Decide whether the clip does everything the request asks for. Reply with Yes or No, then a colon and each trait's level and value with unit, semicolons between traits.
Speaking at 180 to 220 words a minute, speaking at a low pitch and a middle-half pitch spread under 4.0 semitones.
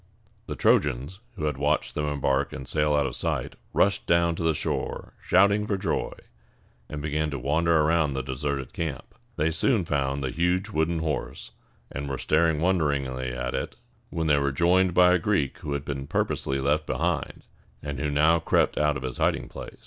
Yes: average, 190 wpm; very low, 75 Hz; average, 3.2 semitones